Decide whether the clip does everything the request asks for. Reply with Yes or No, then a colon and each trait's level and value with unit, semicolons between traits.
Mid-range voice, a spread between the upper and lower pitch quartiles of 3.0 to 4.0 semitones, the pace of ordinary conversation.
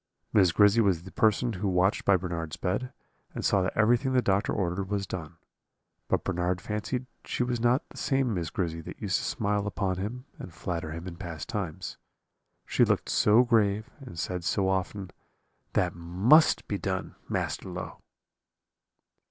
No: very low, 95 Hz; average, 3.4 semitones; average, 170 wpm